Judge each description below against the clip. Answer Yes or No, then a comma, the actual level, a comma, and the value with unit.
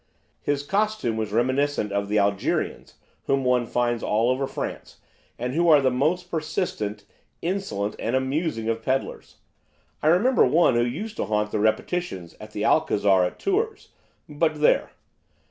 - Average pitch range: No, wide, 7.0 semitones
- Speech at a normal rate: Yes, average, 155 wpm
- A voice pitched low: Yes, low, 130 Hz